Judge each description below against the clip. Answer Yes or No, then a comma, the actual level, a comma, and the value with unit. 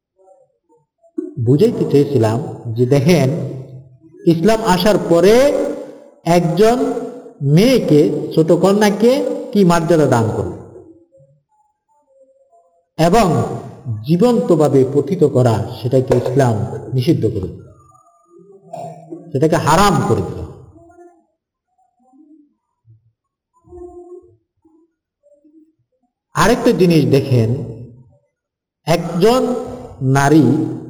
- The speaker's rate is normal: Yes, average, 55 wpm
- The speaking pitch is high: No, medium, 170 Hz